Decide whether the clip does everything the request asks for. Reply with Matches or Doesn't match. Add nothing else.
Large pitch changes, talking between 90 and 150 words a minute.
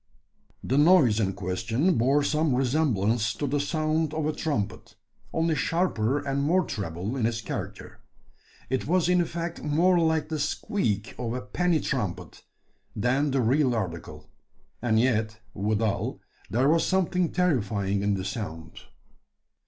Matches